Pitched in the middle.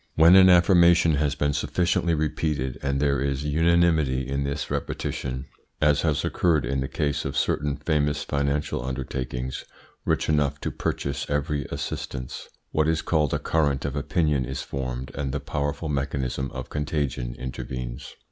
No: very low, 70 Hz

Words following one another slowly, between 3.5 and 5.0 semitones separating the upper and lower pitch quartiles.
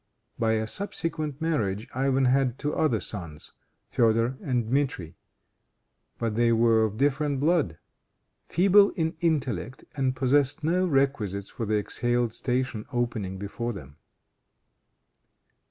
Yes: slow, 120 wpm; average, 4.6 semitones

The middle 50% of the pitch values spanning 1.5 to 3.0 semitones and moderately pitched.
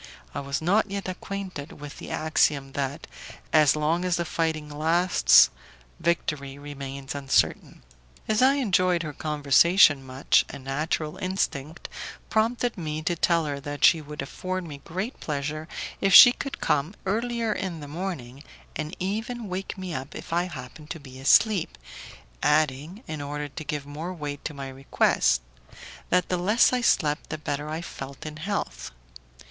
No: average, 4.3 semitones; medium, 155 Hz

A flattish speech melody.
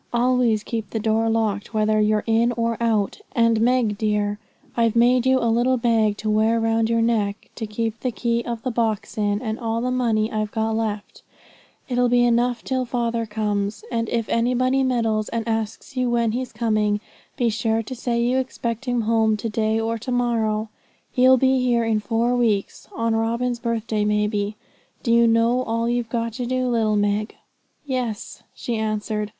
Yes: narrow, 1.9 semitones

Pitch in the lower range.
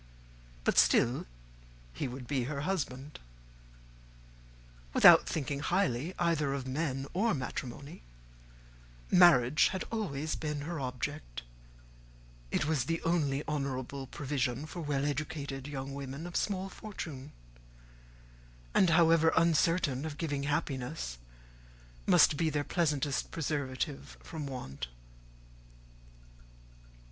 No: medium, 145 Hz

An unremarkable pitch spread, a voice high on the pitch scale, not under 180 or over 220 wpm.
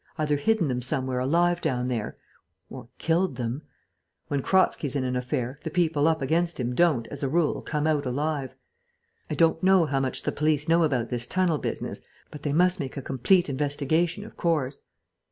No: average, 4.2 semitones; medium, 150 Hz; average, 190 wpm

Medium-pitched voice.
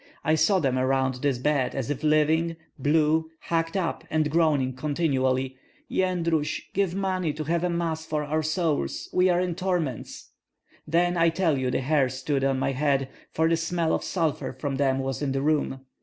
Yes: medium, 155 Hz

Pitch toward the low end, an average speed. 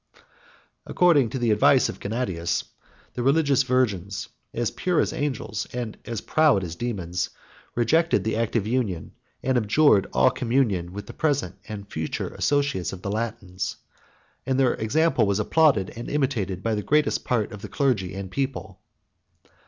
Yes: low, 115 Hz; average, 160 wpm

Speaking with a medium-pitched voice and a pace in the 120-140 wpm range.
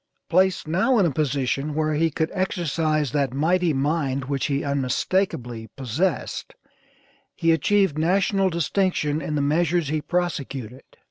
Yes: medium, 155 Hz; slow, 135 wpm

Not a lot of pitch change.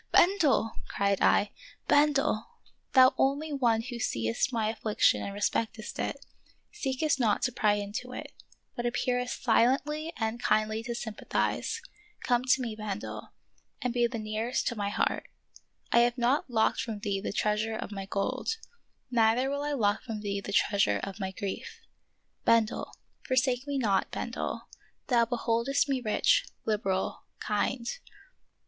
No: average, 3.5 semitones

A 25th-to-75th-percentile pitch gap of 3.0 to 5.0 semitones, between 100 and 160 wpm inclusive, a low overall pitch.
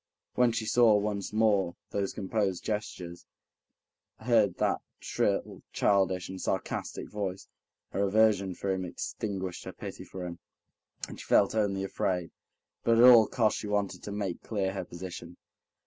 No: narrow, 2.4 semitones; average, 150 wpm; low, 100 Hz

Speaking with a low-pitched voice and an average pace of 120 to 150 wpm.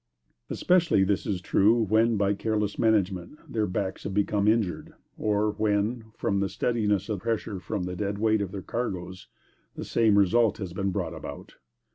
No: low, 105 Hz; average, 170 wpm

